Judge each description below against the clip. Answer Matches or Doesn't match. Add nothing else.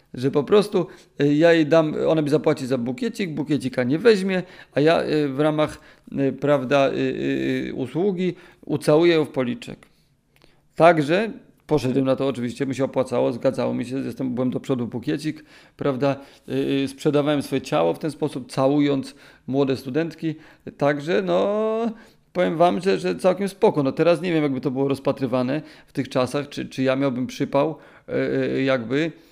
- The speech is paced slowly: Doesn't match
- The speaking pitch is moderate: Matches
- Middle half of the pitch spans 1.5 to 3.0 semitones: Doesn't match